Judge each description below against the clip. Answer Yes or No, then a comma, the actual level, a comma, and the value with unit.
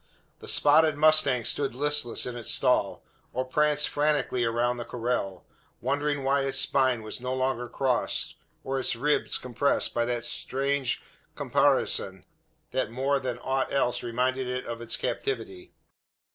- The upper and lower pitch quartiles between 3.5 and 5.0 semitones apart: No, average, 2.7 semitones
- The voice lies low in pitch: Yes, low, 130 Hz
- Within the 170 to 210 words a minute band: No, average, 145 wpm